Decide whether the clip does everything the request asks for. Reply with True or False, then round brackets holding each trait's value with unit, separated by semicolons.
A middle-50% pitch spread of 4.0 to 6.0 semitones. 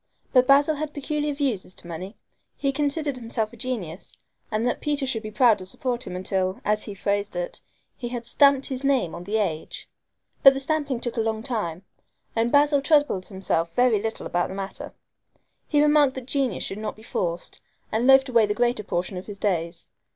True (5.6 semitones)